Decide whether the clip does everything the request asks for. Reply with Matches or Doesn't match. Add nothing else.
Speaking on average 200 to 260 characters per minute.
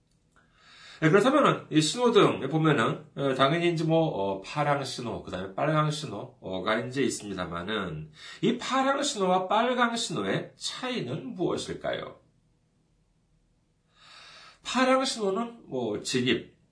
Matches